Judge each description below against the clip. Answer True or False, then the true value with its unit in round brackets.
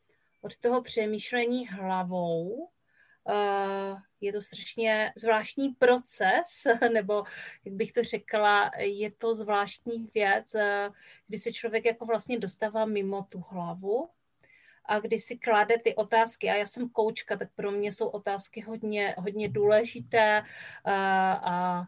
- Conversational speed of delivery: True (135 wpm)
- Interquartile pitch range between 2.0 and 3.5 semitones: True (2.4 semitones)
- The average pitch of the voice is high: True (215 Hz)